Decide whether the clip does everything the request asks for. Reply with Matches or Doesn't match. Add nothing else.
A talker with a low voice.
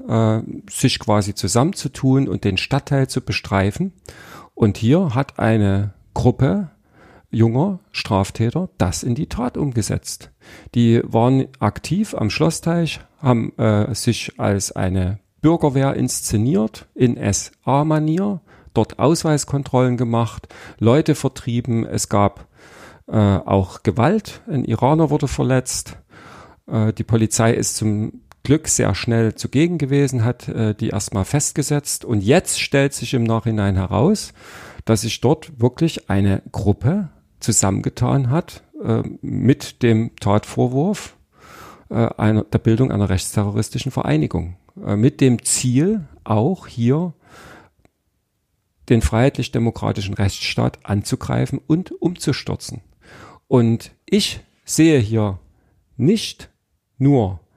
Matches